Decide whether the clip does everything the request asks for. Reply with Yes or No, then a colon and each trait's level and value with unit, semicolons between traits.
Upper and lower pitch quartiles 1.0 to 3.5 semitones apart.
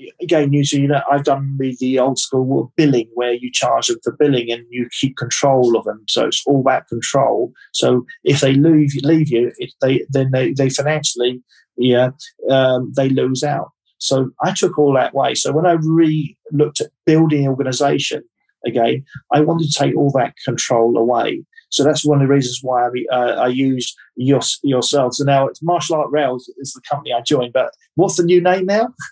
Yes: average, 3.2 semitones